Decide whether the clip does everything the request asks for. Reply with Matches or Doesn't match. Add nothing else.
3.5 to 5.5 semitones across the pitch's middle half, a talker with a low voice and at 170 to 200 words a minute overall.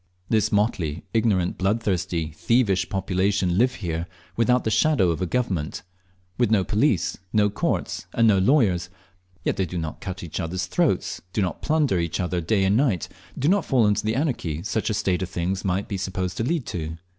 Matches